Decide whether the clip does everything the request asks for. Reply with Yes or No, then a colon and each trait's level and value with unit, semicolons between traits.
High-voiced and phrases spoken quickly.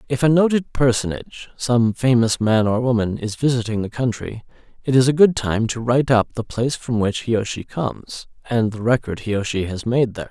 No: low, 120 Hz; fast, 220 wpm